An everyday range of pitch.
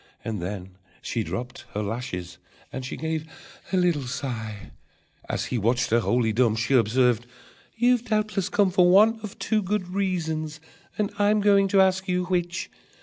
No: wide, 8.6 semitones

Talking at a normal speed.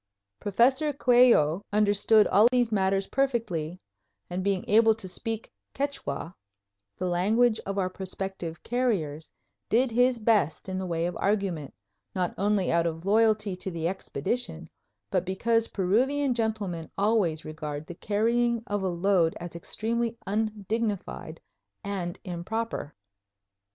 No: slow, 130 wpm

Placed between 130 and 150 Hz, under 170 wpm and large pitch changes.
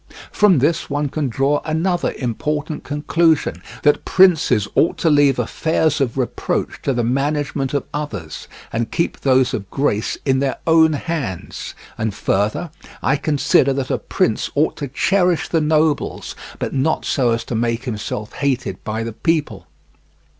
No: medium, 140 Hz; average, 155 wpm; average, 4.5 semitones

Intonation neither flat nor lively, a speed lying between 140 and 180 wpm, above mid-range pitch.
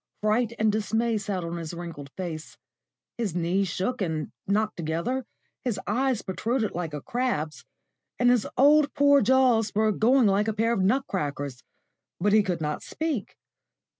No: wide, 5.8 semitones; average, 165 wpm; high, 210 Hz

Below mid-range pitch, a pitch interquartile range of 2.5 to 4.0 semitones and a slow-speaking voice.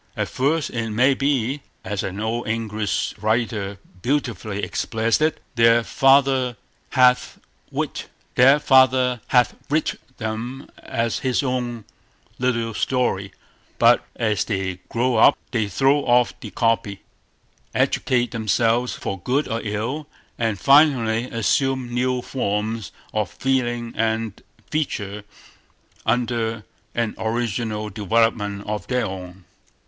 Yes: low, 115 Hz; average, 2.9 semitones; slow, 110 wpm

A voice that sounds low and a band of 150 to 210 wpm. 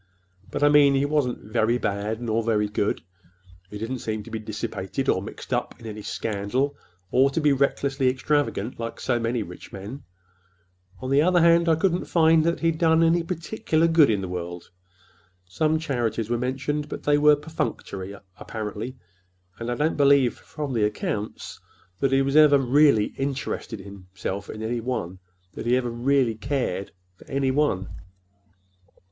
Yes: low, 130 Hz; average, 165 wpm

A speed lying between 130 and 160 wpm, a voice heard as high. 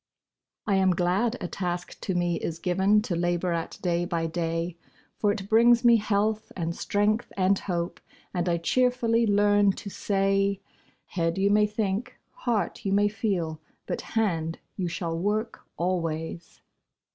Yes: average, 155 wpm; high, 195 Hz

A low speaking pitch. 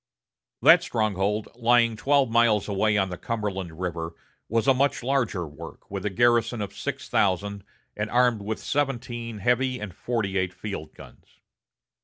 Yes: low, 110 Hz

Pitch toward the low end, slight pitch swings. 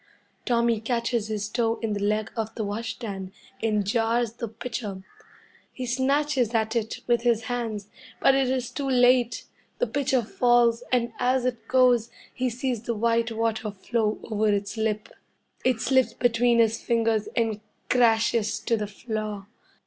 No: high, 230 Hz; narrow, 2.1 semitones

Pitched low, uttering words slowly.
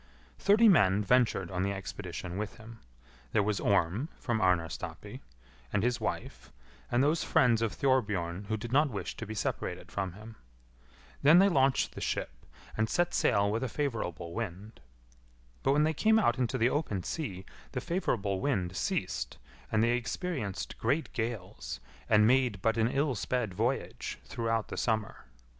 No: low, 115 Hz; average, 165 wpm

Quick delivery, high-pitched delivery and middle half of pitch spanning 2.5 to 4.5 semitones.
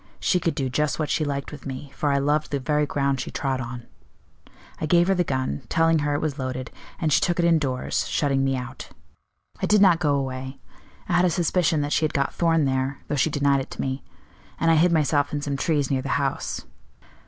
No: fast, 235 wpm; medium, 145 Hz; average, 3.0 semitones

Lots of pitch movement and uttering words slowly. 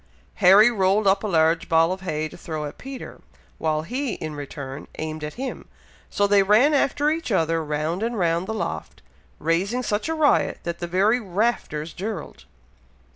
No: wide, 5.7 semitones; average, 180 wpm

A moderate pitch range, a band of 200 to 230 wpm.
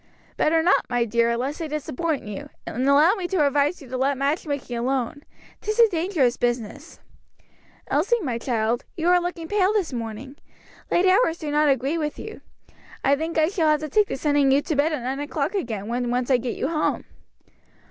Yes: average, 4.7 semitones; fast, 205 wpm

